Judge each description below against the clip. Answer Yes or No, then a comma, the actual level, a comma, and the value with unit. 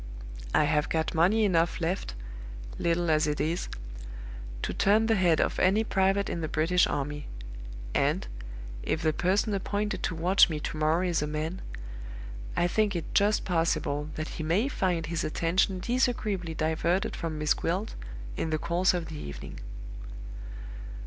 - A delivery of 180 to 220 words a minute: No, average, 160 wpm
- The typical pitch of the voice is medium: Yes, medium, 170 Hz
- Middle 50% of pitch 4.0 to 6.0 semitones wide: No, average, 3.4 semitones